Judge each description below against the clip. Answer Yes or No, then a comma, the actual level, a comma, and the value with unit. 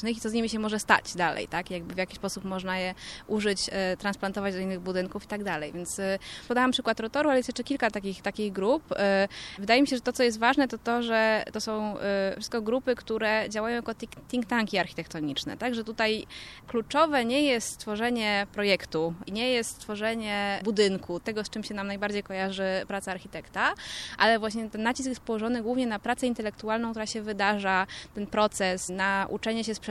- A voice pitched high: Yes, high, 215 Hz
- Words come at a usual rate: No, fast, 200 wpm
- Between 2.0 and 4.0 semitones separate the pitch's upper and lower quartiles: Yes, average, 2.9 semitones